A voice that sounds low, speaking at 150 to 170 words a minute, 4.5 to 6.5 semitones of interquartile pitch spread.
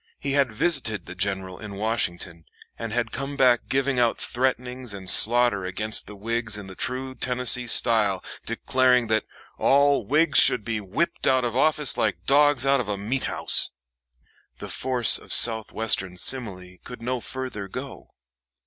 No: low, 120 Hz; average, 165 wpm; average, 4.0 semitones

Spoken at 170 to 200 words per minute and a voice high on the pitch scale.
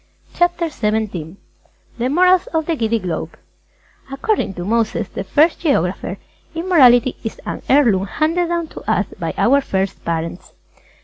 No: average, 145 wpm; high, 240 Hz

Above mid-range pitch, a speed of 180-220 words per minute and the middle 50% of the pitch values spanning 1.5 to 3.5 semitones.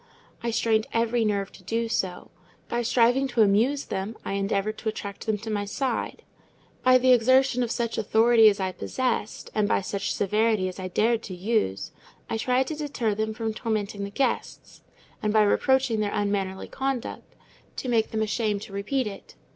Yes: high, 220 Hz; average, 185 wpm; average, 2.9 semitones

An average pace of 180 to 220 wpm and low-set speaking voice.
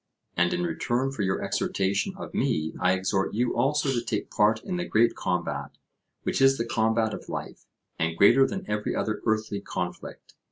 Yes: average, 185 wpm; low, 110 Hz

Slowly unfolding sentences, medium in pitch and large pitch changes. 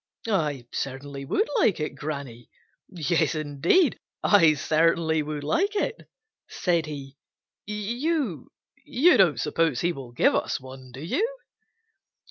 Yes: slow, 120 wpm; medium, 155 Hz; wide, 6.6 semitones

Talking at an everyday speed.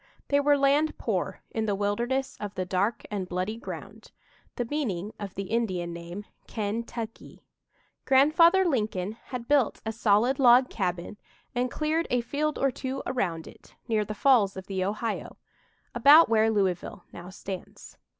Yes: average, 160 wpm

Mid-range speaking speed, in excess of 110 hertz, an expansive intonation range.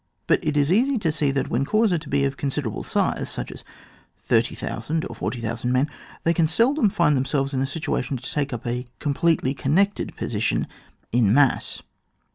No: average, 175 wpm; medium, 140 Hz; average, 4.2 semitones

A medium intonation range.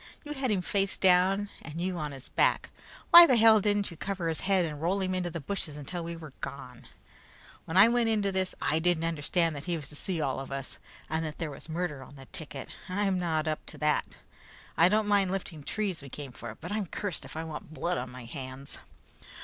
Yes: average, 4.5 semitones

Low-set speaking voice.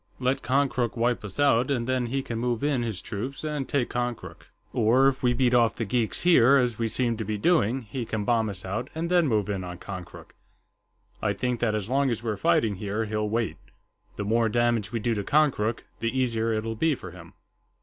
Yes: low, 115 Hz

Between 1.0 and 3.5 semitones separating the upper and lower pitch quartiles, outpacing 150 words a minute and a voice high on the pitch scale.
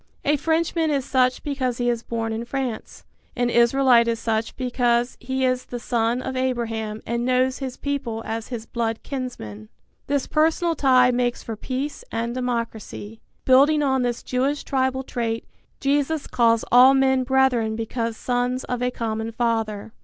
Yes: narrow, 2.5 semitones; average, 160 wpm; very high, 250 Hz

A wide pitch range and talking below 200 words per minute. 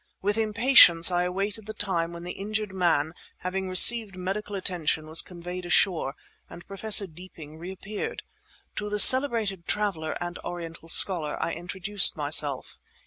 No: average, 3.5 semitones; average, 140 wpm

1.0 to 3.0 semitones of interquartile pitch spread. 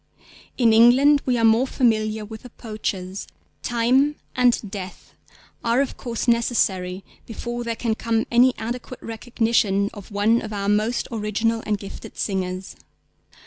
Yes: narrow, 2.6 semitones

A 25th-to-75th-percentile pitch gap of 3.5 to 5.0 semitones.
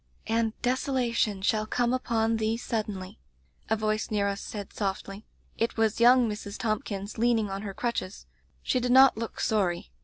No: narrow, 2.4 semitones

